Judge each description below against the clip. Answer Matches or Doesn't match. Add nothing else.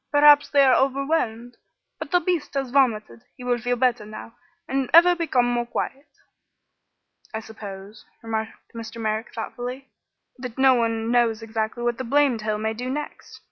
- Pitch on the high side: Matches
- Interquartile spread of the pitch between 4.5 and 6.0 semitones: Doesn't match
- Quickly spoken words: Doesn't match